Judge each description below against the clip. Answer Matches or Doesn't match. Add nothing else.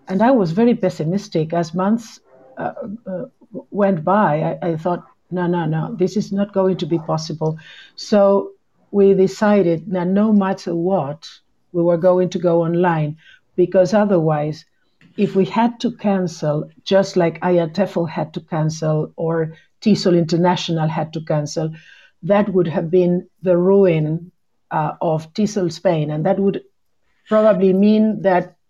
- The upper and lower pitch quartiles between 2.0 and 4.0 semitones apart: Matches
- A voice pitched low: Doesn't match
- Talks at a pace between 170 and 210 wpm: Doesn't match